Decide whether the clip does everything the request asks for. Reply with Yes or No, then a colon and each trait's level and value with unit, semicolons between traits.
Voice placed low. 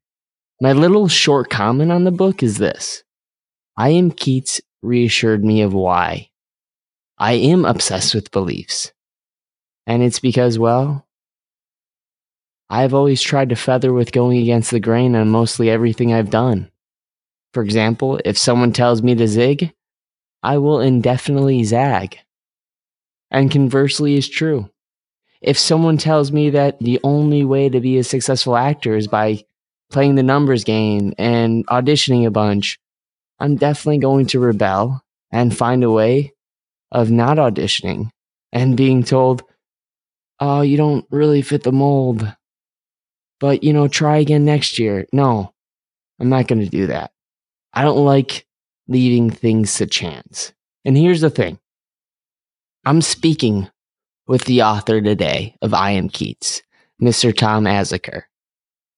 Yes: low, 125 Hz